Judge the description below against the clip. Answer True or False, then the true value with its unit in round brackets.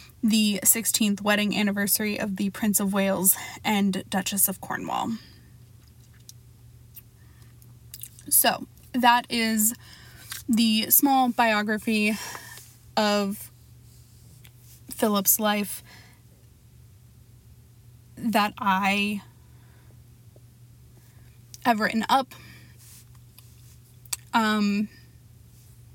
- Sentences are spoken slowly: True (65 wpm)